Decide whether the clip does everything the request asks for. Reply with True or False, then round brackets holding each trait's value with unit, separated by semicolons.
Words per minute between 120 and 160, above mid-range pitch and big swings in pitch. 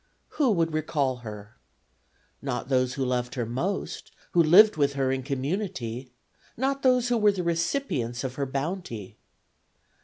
False (150 wpm; 140 Hz; 6.8 semitones)